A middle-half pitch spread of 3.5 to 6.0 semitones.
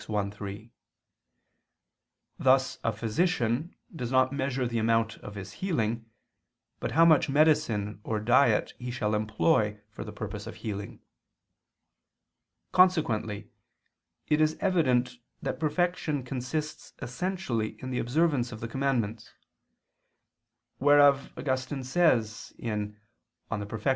Yes: average, 5.0 semitones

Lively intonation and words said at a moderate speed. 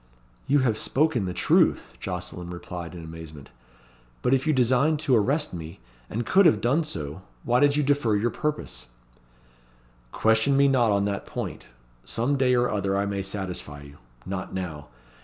Yes: wide, 7.2 semitones; average, 170 wpm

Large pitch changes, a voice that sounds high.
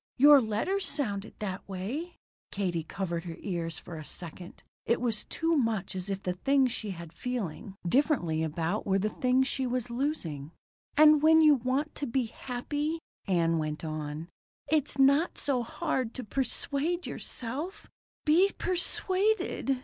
Yes: wide, 8.1 semitones; high, 240 Hz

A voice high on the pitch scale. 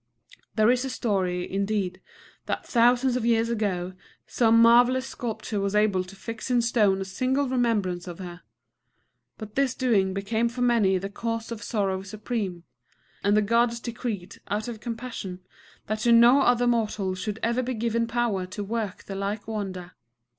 Yes: high, 220 Hz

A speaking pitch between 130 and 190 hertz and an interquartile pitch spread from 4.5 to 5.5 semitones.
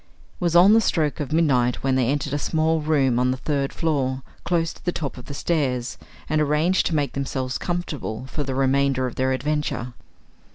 No: medium, 140 Hz; average, 3.3 semitones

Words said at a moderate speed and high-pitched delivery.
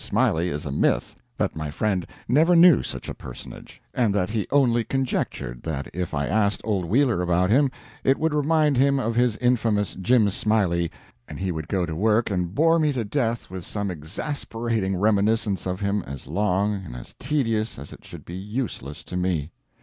No: average, 190 wpm; low, 105 Hz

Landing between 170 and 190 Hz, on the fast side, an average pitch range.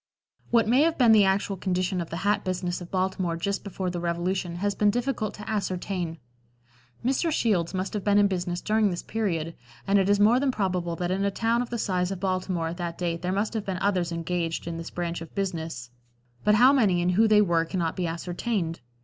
Yes: medium, 185 Hz; fast, 225 wpm; average, 3.1 semitones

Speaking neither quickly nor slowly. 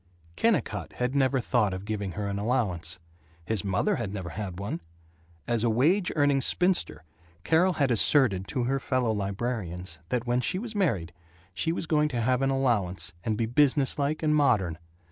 Yes: average, 180 wpm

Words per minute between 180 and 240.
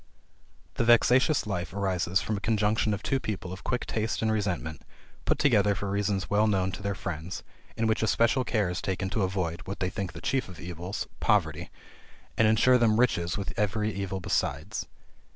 Yes: average, 190 wpm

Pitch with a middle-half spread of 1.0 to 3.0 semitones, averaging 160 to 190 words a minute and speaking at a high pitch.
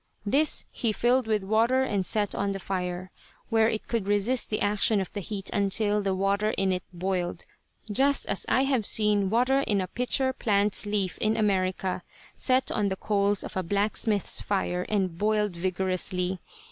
Yes: narrow, 2.5 semitones; average, 175 wpm; high, 205 Hz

